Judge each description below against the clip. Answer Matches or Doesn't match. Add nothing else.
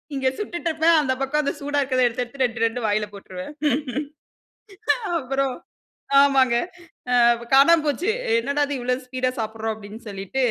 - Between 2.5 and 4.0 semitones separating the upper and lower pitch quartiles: Matches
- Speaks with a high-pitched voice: Matches